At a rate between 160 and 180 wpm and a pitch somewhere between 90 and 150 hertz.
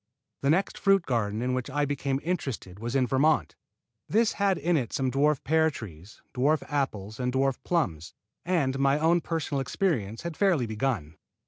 Yes: average, 175 wpm; low, 135 Hz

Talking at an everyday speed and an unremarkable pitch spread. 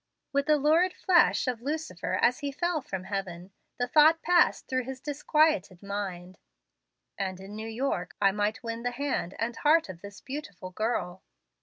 No: average, 170 wpm; wide, 7.2 semitones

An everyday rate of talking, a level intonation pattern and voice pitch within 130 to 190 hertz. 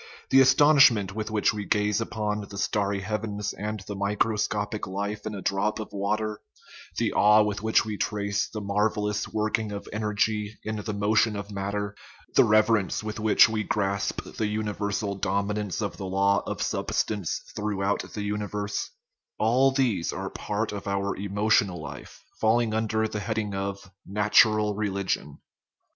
No: average, 160 wpm; narrow, 1.3 semitones; low, 105 Hz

